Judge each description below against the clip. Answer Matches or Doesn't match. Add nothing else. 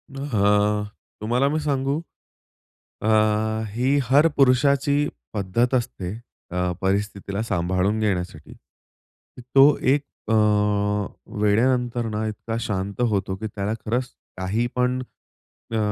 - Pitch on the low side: Matches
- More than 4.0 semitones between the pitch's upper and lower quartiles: Matches